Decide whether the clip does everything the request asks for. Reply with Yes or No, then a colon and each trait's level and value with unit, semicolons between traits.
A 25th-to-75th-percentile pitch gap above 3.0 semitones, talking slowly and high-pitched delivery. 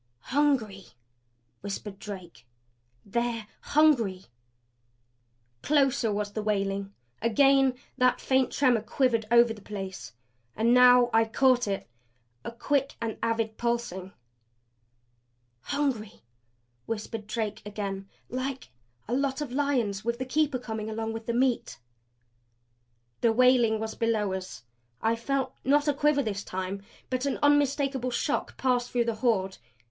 Yes: average, 3.8 semitones; slow, 125 wpm; high, 235 Hz